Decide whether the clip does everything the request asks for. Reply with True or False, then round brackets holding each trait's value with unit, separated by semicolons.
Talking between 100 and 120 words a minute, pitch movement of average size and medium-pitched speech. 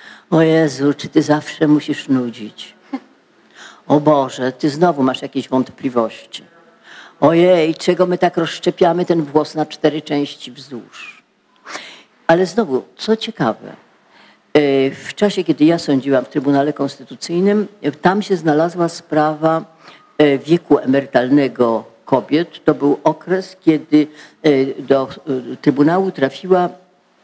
True (110 wpm; 3.9 semitones; 150 Hz)